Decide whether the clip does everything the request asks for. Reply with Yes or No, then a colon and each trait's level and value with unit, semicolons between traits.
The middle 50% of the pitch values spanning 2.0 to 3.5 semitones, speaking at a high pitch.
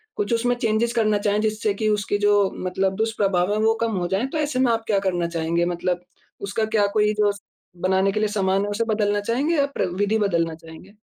Yes: average, 2.8 semitones; high, 205 Hz